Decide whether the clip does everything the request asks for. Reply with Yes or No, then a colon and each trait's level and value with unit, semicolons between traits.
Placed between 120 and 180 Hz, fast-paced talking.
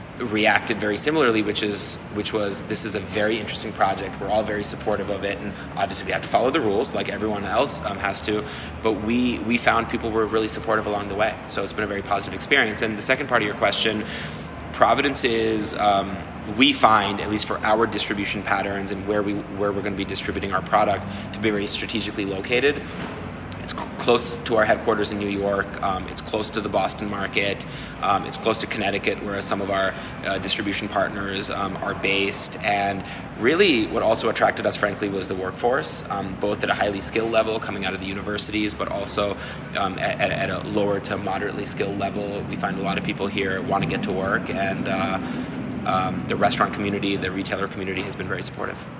No: low, 100 Hz; fast, 210 wpm